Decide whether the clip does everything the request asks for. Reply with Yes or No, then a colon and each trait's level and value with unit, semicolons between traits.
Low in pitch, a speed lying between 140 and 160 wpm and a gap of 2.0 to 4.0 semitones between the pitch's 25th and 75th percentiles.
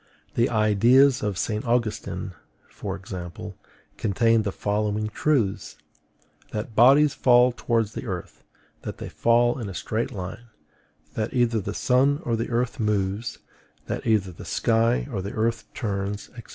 Yes: low, 110 Hz; average, 150 wpm; average, 2.8 semitones